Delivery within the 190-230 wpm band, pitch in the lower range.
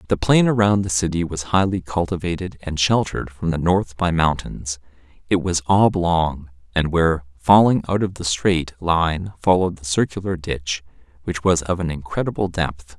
No: average, 165 wpm; very low, 85 Hz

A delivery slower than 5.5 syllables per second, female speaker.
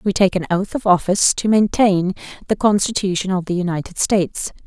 No: 5.6 syllables/s; female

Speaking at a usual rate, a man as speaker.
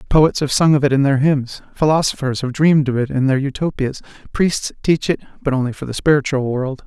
No: fast, 220 wpm; male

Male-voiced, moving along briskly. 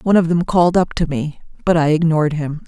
No: female; fast, 245 wpm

